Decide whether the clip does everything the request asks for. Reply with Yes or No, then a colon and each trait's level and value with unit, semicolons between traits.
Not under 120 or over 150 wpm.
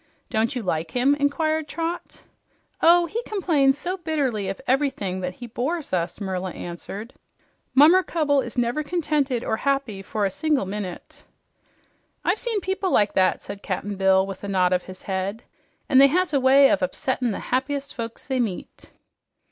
No: average, 170 wpm